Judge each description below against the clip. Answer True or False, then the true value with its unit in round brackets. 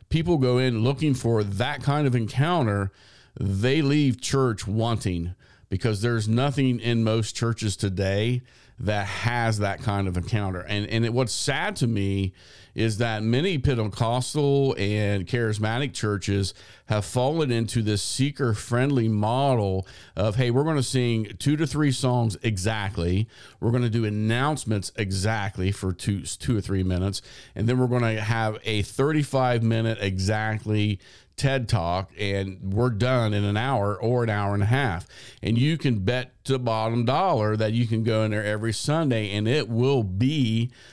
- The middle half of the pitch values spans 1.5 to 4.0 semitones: True (3.6 semitones)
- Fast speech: False (165 wpm)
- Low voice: True (115 Hz)